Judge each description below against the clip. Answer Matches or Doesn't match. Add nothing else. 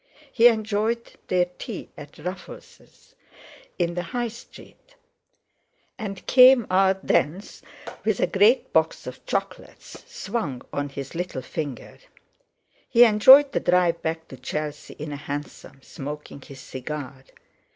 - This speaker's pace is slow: Matches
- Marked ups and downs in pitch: Matches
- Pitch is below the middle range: Doesn't match